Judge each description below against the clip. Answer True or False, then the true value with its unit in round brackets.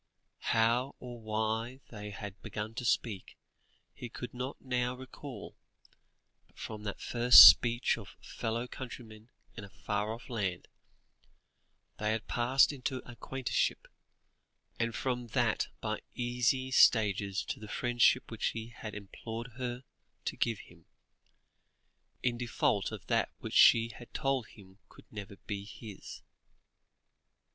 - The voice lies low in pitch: True (115 Hz)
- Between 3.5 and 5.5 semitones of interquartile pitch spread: False (2.5 semitones)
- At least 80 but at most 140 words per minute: True (135 wpm)